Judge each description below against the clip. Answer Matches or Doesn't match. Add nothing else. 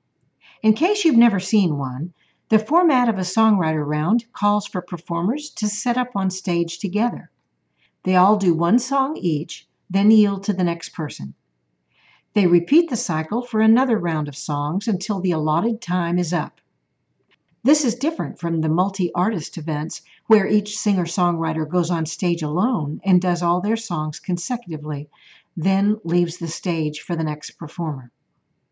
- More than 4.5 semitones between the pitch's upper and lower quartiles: Matches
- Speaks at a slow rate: Doesn't match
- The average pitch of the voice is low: Doesn't match